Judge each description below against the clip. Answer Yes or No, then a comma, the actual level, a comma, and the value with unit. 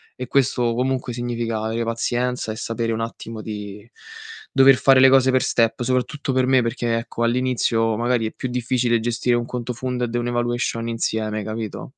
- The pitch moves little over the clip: Yes, narrow, 1.7 semitones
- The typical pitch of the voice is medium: No, low, 120 Hz